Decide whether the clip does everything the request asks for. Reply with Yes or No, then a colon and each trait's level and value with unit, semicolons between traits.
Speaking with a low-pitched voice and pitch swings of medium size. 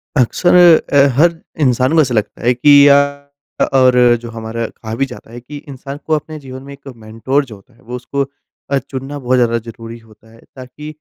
Yes: low, 130 Hz; average, 3.2 semitones